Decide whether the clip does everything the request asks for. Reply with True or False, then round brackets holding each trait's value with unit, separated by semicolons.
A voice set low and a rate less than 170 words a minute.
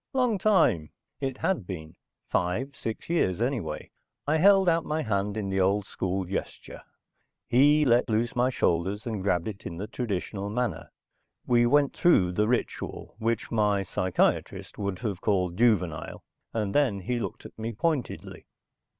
True (110 Hz; 160 wpm)